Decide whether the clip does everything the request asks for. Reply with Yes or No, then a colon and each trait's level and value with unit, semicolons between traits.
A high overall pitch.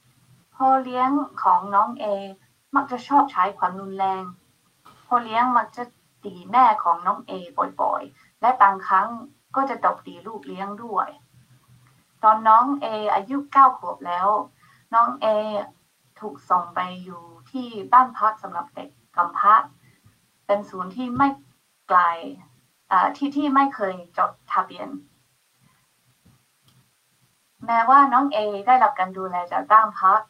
Yes: high, 210 Hz